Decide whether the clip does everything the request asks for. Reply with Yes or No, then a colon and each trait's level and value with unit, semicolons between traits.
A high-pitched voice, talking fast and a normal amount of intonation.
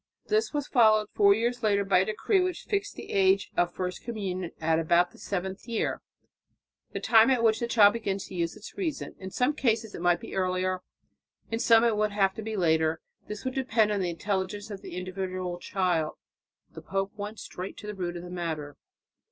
Yes: high, 200 Hz; fast, 210 wpm; average, 3.6 semitones